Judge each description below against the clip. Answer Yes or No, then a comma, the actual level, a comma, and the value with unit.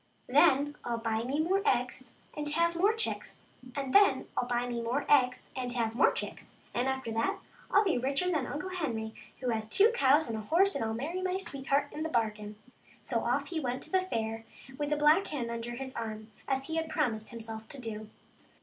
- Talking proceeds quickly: Yes, fast, 215 wpm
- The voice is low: No, very high, 265 Hz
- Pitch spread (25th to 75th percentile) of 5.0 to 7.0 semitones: Yes, average, 5.3 semitones